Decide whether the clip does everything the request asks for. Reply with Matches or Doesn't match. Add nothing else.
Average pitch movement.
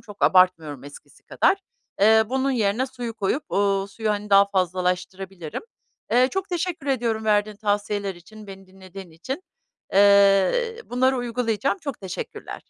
Matches